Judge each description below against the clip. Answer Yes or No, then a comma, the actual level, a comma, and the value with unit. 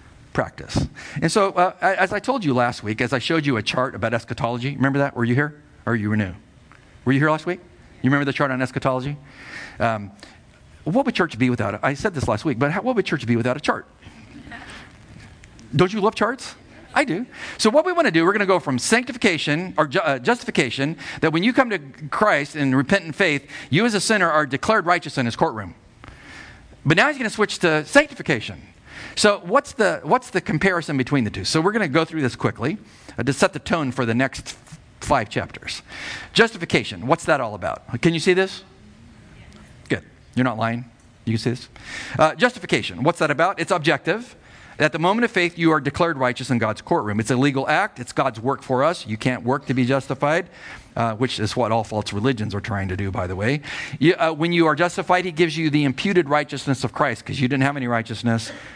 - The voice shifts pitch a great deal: Yes, wide, 6.5 semitones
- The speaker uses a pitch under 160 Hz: Yes, medium, 145 Hz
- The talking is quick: Yes, fast, 225 wpm